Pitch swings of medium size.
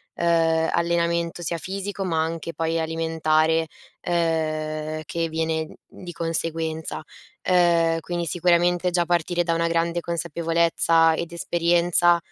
No: narrow, 1.0 semitones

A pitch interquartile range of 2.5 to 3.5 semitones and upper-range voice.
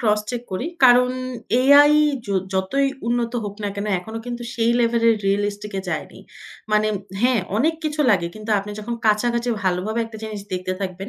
Yes: average, 3.1 semitones; high, 220 Hz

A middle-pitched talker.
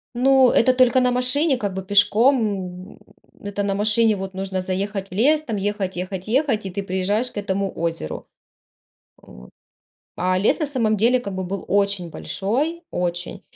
No: high, 205 Hz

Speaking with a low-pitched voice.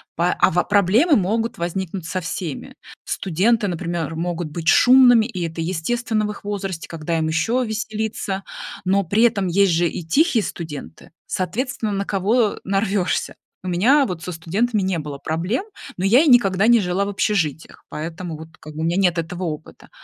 No: high, 190 Hz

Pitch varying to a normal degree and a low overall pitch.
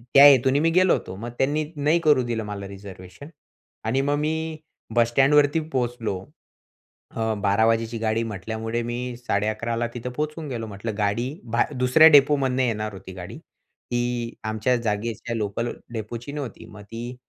Yes: average, 3.5 semitones; low, 120 Hz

